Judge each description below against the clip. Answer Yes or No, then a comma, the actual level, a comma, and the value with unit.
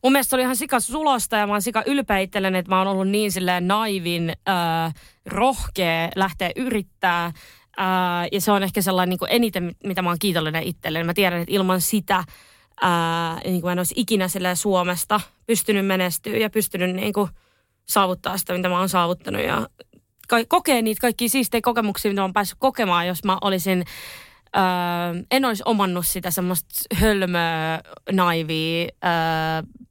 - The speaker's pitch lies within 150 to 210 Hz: Yes, high, 190 Hz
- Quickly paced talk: Yes, fast, 160 wpm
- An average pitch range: Yes, average, 3.2 semitones